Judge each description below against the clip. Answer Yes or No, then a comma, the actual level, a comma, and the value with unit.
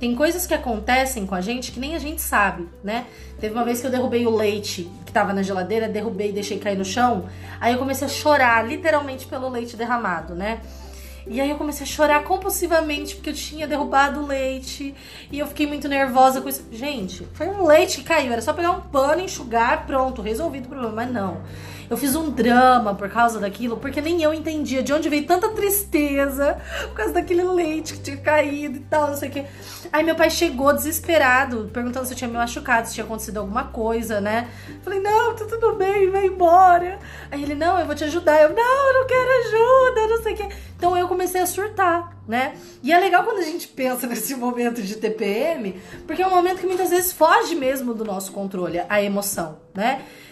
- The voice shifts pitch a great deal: Yes, wide, 6.2 semitones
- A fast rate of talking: Yes, fast, 215 wpm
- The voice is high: Yes, very high, 280 Hz